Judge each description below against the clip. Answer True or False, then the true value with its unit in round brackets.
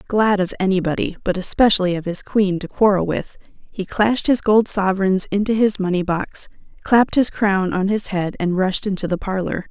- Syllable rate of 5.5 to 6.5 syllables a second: False (5.2 syllables/s)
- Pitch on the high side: True (195 Hz)